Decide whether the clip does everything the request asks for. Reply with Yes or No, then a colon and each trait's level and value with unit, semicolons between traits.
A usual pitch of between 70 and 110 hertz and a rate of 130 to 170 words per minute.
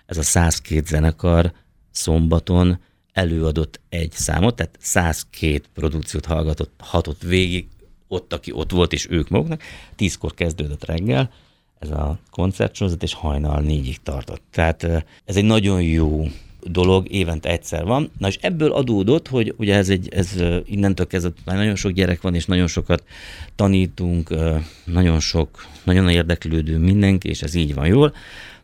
Yes: very low, 85 Hz; average, 145 wpm